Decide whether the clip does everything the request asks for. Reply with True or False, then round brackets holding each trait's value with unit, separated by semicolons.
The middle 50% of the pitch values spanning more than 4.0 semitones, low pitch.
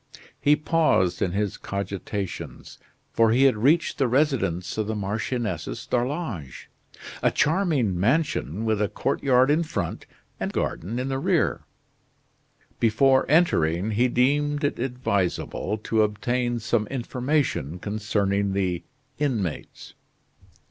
True (5.3 semitones; 115 Hz)